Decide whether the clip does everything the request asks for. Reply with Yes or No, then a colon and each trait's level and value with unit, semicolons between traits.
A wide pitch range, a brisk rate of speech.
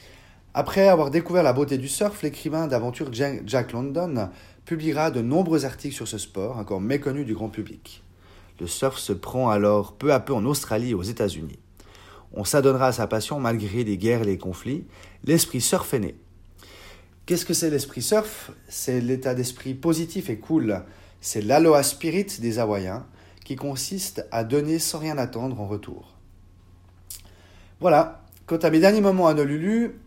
No: wide, 7.1 semitones; average, 170 wpm